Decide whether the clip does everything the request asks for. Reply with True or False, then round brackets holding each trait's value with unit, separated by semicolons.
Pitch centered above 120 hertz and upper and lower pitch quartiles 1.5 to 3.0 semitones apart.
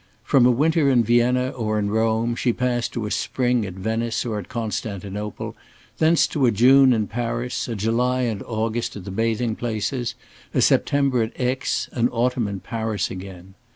False (115 Hz; 2.6 semitones)